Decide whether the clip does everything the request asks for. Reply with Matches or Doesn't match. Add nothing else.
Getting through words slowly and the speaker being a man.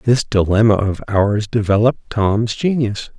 Matches